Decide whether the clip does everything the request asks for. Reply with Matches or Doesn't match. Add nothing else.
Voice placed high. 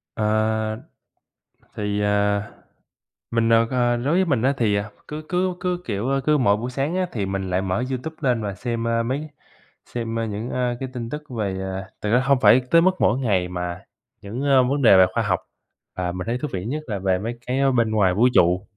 Doesn't match